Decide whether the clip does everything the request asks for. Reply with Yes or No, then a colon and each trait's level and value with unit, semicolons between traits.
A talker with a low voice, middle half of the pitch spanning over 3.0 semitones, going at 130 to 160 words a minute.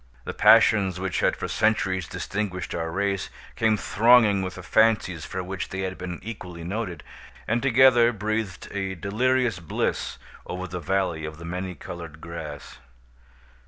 Yes: very low, 95 Hz; average, 3.7 semitones; average, 155 wpm